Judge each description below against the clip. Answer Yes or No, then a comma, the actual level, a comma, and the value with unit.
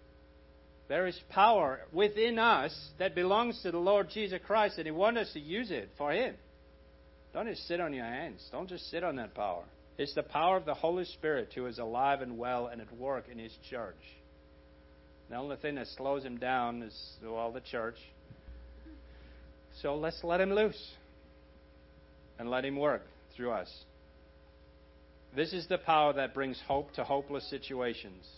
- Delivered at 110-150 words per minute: No, average, 180 wpm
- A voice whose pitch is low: Yes, low, 120 Hz